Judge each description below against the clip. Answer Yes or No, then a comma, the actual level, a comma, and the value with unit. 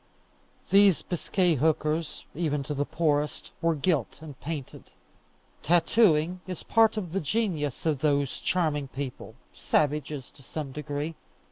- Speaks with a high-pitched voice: No, medium, 155 Hz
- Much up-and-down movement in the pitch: No, average, 3.3 semitones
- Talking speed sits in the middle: No, slow, 130 wpm